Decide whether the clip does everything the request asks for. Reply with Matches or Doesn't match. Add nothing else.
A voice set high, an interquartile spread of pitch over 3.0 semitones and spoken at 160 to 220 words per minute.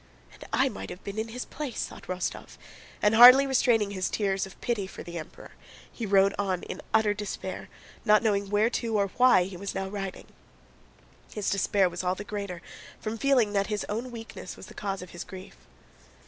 Doesn't match